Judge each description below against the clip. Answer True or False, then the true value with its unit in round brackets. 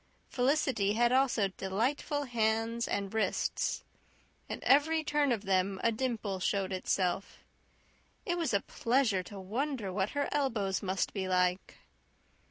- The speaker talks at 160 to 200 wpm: False (135 wpm)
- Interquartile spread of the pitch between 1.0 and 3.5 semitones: False (5.6 semitones)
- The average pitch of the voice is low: False (220 Hz)